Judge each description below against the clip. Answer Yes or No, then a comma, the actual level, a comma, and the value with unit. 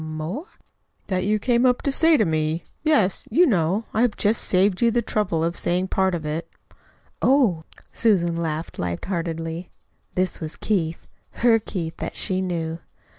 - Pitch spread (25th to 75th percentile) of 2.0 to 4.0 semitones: No, average, 5.2 semitones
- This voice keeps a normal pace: Yes, average, 175 wpm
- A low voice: No, medium, 185 Hz